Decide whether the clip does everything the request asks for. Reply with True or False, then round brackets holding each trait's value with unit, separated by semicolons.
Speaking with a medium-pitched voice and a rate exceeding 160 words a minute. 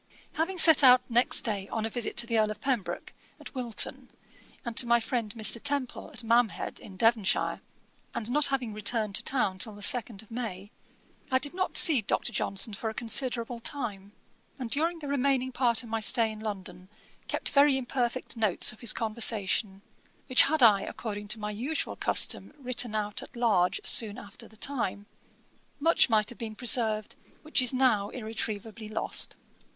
False (230 Hz; 180 wpm)